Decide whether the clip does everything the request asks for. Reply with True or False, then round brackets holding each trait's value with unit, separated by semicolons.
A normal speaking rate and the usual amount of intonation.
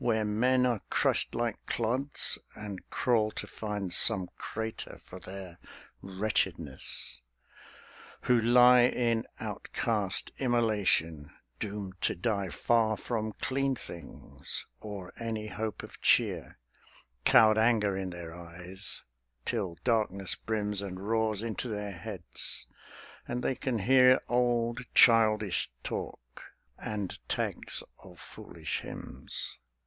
False (115 wpm; 3.5 semitones)